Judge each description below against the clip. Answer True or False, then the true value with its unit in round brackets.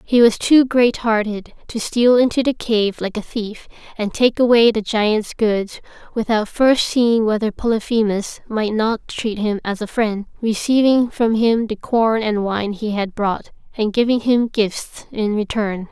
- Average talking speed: True (175 wpm)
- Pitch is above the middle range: True (220 Hz)